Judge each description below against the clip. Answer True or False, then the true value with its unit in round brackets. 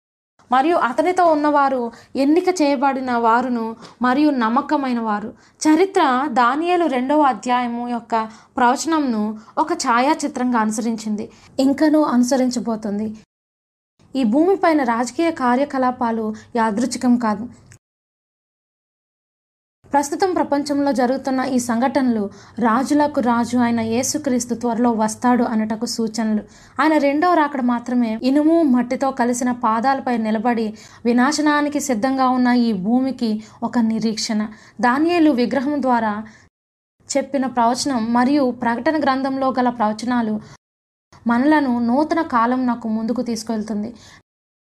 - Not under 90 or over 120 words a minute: True (100 wpm)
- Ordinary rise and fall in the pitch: True (3.5 semitones)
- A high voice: True (245 Hz)